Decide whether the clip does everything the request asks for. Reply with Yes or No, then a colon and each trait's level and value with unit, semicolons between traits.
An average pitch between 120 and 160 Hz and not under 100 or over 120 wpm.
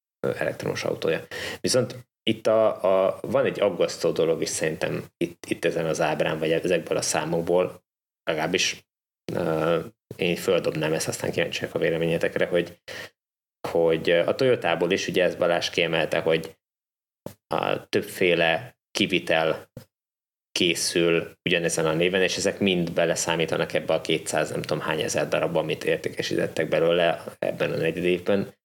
No: low, 125 Hz; average, 140 wpm